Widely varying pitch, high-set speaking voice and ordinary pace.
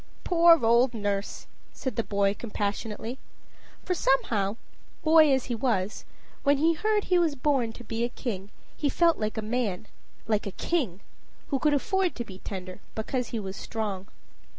Yes: wide, 5.9 semitones; high, 235 Hz; average, 170 wpm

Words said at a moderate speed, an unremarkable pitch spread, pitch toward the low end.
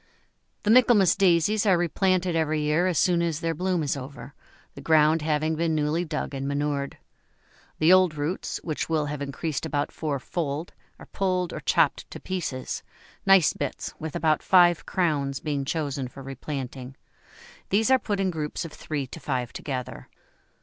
No: average, 165 wpm; average, 3.7 semitones; medium, 155 Hz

